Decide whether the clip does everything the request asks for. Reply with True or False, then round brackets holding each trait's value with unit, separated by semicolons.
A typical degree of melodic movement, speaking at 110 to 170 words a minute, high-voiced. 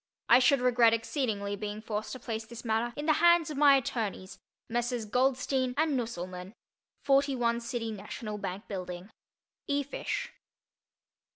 True (4.1 semitones; 145 wpm; 235 Hz)